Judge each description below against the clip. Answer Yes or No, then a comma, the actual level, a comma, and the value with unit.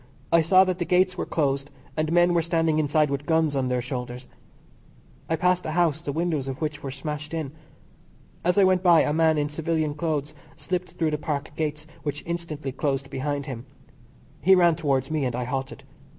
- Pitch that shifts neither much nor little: Yes, average, 3.2 semitones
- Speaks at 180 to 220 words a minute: Yes, average, 200 wpm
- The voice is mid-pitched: Yes, medium, 155 Hz